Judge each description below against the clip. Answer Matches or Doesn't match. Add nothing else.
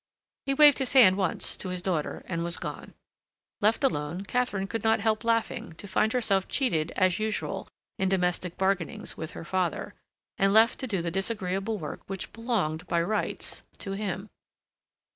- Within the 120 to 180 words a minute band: Matches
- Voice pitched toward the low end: Doesn't match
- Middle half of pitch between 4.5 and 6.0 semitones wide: Doesn't match